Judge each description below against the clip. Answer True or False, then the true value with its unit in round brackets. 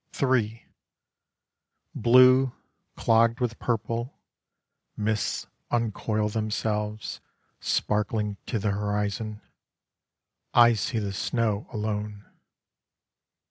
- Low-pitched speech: True (110 Hz)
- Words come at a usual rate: False (75 wpm)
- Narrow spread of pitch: True (1.9 semitones)